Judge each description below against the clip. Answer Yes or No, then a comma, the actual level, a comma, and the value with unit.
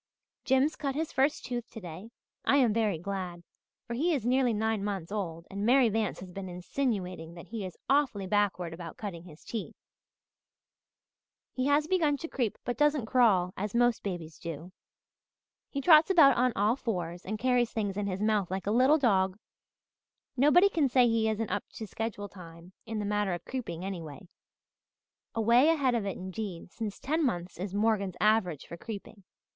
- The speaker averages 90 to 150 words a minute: No, average, 180 wpm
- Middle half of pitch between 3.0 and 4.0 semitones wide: No, average, 5.3 semitones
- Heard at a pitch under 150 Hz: No, high, 215 Hz